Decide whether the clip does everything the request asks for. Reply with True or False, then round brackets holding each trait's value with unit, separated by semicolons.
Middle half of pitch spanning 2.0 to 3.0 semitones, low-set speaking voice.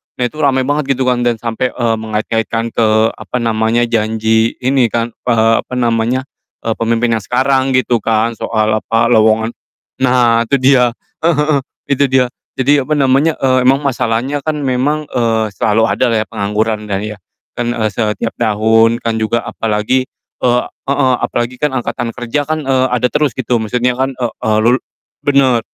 True (2.7 semitones; 120 Hz)